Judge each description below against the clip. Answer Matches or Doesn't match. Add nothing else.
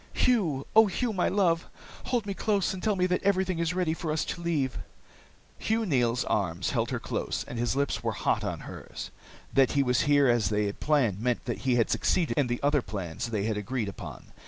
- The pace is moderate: Doesn't match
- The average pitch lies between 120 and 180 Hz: Matches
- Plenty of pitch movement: Matches